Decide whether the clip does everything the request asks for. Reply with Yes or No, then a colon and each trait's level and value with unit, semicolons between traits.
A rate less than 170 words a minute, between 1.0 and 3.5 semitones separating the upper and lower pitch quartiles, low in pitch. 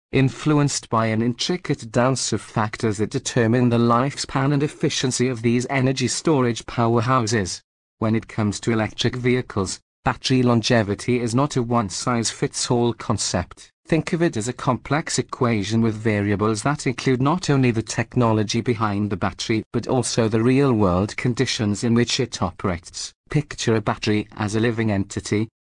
Yes: average, 160 wpm; average, 3.0 semitones; low, 120 Hz